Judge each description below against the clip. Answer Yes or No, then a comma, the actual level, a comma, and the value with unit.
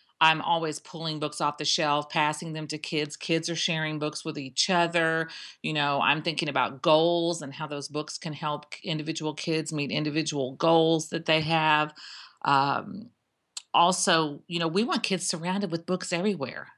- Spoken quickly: No, average, 175 wpm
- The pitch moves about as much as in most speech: No, narrow, 2.0 semitones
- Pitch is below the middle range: No, medium, 160 Hz